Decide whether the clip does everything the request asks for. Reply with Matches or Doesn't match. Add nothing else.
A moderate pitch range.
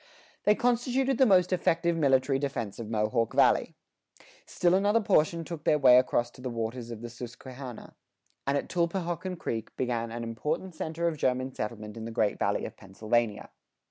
Doesn't match